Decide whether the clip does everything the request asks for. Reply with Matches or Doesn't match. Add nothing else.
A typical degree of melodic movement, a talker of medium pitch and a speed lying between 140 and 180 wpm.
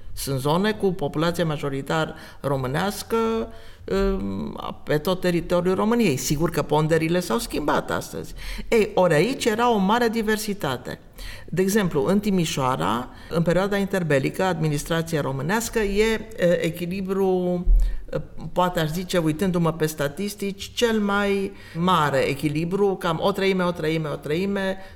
Doesn't match